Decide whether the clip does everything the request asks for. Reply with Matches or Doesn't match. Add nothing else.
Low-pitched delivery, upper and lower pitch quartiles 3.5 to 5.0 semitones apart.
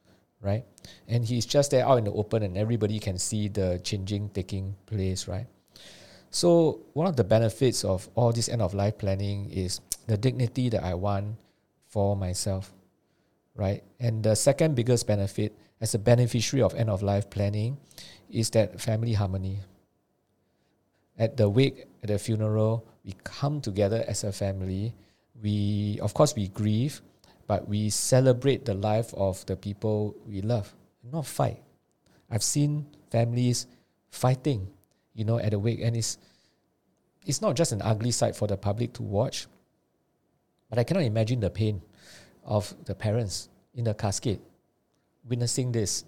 Doesn't match